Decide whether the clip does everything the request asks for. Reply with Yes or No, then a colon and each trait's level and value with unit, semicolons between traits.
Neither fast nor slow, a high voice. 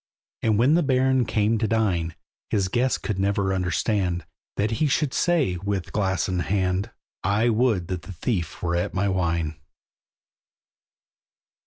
No: average, 145 wpm; low, 100 Hz